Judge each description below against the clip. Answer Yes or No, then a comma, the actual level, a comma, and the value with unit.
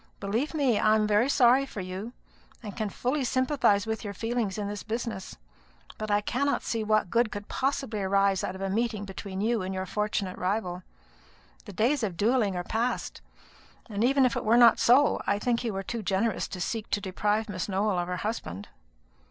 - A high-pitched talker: Yes, high, 215 Hz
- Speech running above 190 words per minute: Yes, average, 200 wpm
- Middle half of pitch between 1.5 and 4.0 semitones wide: Yes, average, 3.3 semitones